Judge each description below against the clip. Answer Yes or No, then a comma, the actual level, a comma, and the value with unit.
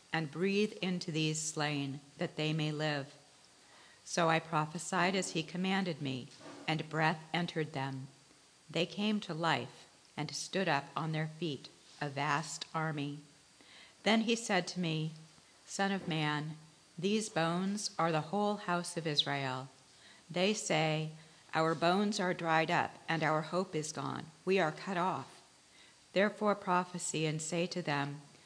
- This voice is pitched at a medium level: Yes, medium, 160 Hz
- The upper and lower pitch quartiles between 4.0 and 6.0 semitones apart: No, average, 2.9 semitones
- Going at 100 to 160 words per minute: Yes, average, 150 wpm